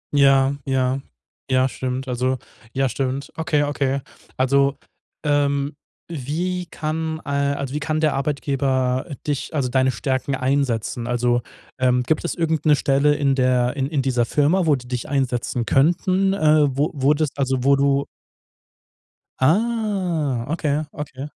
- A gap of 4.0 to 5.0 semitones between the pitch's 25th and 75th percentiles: No, narrow, 2.6 semitones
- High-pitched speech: No, medium, 140 Hz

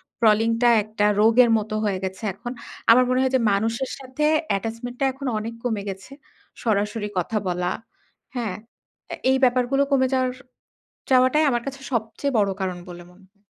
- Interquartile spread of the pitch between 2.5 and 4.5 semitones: Yes, average, 3.6 semitones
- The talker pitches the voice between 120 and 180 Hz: No, high, 230 Hz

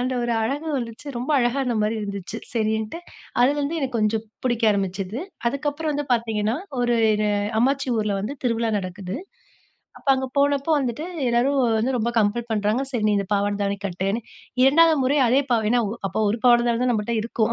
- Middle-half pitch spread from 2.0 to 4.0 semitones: Yes, average, 3.7 semitones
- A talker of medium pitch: No, high, 235 Hz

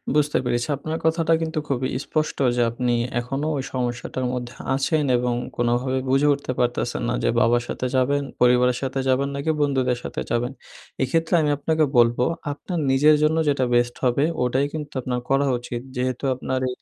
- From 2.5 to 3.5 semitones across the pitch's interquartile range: Yes, average, 2.9 semitones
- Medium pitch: No, low, 130 Hz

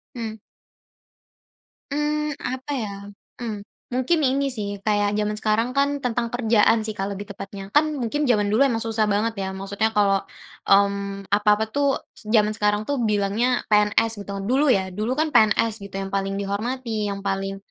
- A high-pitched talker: Yes, high, 215 Hz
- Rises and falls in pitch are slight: No, average, 3.4 semitones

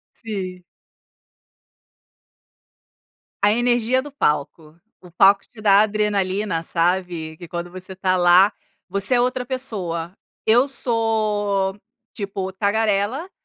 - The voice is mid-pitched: No, high, 200 Hz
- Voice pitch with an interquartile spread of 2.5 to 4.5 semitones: Yes, average, 3.6 semitones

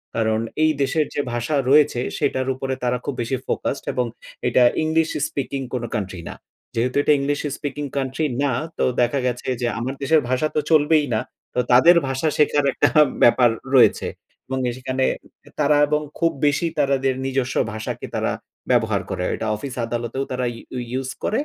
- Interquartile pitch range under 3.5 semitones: Yes, average, 2.9 semitones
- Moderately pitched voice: No, low, 130 Hz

